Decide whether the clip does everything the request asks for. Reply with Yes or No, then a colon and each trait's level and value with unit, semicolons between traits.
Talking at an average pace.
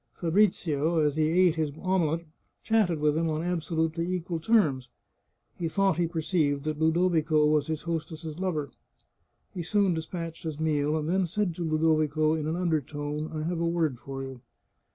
Yes: average, 175 wpm